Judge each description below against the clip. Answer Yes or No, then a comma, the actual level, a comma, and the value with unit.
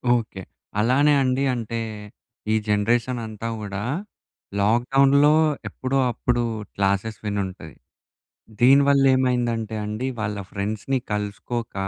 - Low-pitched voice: Yes, low, 115 Hz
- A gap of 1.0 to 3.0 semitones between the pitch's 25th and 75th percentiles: No, average, 3.8 semitones